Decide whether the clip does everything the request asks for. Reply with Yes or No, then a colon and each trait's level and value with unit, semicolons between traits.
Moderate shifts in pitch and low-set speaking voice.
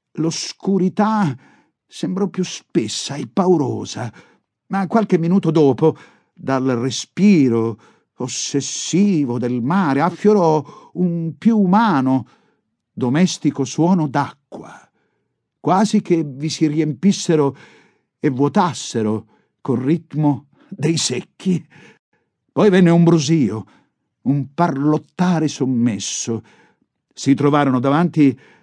No: average, 4.9 semitones; medium, 155 Hz